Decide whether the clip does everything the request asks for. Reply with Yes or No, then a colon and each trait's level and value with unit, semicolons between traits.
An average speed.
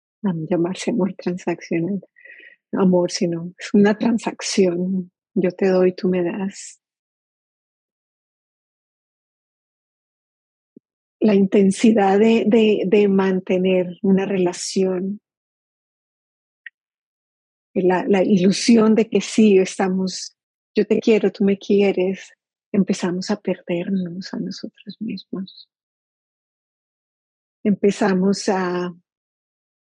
No: slow, 90 wpm